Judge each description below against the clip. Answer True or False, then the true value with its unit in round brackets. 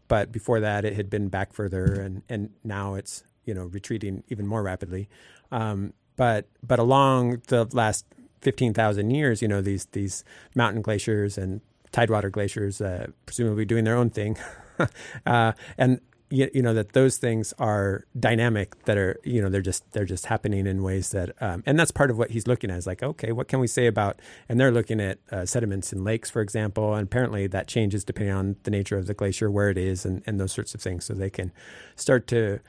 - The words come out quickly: True (210 wpm)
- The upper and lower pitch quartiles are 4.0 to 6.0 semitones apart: False (3.2 semitones)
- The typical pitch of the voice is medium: False (105 Hz)